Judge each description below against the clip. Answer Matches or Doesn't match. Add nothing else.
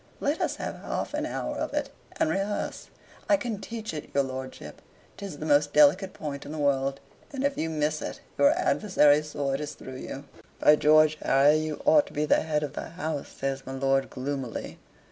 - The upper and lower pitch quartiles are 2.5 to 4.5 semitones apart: Doesn't match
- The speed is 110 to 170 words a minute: Doesn't match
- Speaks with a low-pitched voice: Doesn't match